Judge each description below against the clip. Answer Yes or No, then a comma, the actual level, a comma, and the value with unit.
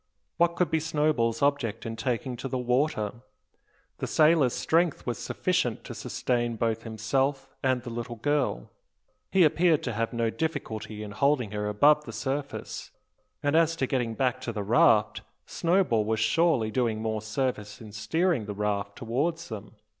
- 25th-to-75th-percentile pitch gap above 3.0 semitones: Yes, average, 5.1 semitones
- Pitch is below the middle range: Yes, low, 125 Hz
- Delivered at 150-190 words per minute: Yes, average, 165 wpm